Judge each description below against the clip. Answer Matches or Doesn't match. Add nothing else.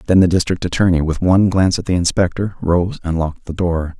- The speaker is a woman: Doesn't match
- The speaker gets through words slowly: Doesn't match